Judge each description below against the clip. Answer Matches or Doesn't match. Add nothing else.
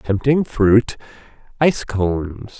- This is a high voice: Doesn't match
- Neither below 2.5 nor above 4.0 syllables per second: Matches